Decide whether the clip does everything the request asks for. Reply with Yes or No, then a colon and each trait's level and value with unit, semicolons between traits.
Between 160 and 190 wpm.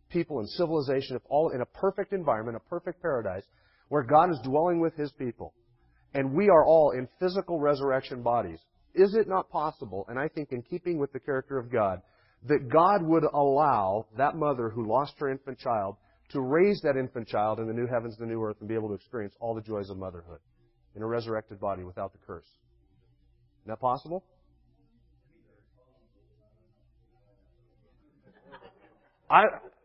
Yes: average, 175 wpm